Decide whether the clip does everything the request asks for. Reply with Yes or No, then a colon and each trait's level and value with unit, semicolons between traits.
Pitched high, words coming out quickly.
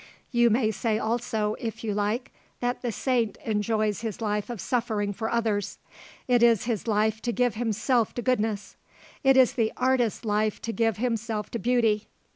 No: high, 225 Hz; average, 175 wpm